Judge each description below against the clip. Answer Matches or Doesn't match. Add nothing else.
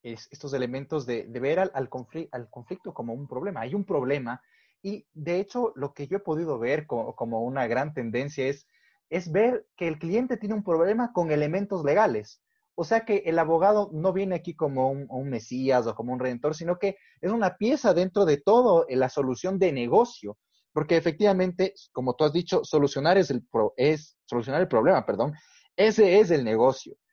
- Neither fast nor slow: Doesn't match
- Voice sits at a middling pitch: Matches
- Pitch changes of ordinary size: Doesn't match